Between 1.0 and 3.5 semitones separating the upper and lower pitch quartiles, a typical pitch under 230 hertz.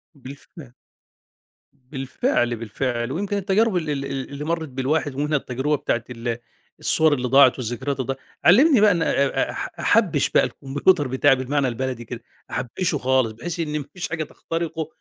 No: average, 3.9 semitones; medium, 140 Hz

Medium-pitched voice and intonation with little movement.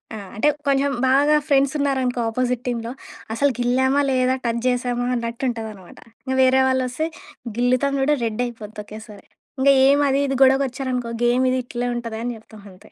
No: very high, 250 Hz; narrow, 2.3 semitones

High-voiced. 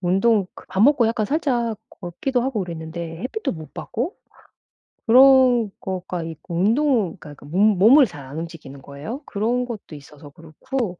Yes: high, 195 Hz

